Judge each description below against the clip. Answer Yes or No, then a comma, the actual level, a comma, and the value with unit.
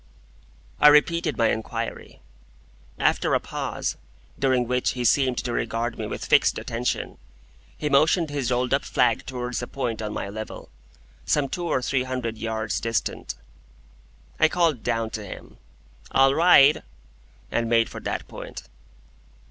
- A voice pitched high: No, low, 125 Hz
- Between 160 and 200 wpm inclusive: No, average, 150 wpm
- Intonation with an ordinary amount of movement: Yes, average, 3.5 semitones